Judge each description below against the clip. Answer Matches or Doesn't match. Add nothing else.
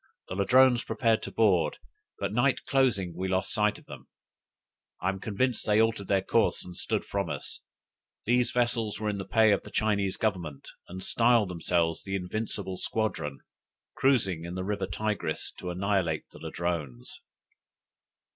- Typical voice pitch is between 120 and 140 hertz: Doesn't match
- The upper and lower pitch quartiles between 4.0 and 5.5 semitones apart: Doesn't match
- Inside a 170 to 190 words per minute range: Doesn't match